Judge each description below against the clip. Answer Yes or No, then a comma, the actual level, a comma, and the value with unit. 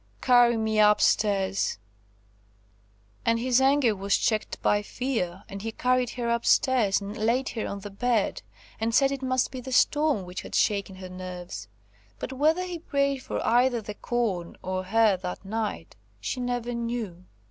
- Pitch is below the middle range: No, high, 225 Hz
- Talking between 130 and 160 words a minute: No, average, 170 wpm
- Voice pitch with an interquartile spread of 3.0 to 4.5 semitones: Yes, average, 4.2 semitones